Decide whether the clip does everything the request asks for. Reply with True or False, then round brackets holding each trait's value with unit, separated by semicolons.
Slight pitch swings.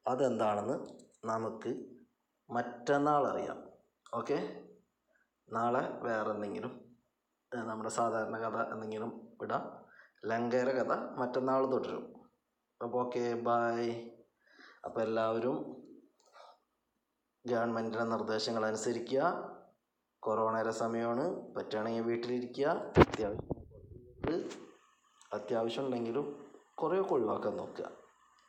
True (1.7 semitones)